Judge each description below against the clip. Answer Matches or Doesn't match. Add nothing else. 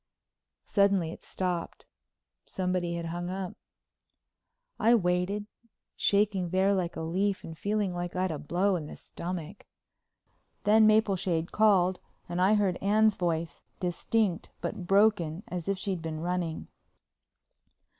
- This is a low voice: Doesn't match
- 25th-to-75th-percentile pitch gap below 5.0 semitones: Matches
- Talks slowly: Matches